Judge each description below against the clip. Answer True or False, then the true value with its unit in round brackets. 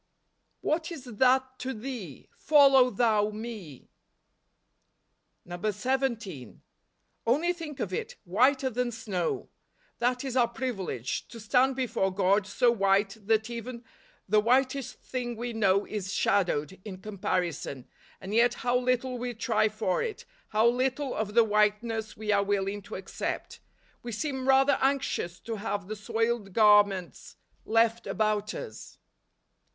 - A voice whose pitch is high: True (225 Hz)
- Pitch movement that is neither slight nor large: True (3.9 semitones)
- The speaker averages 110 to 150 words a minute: True (140 wpm)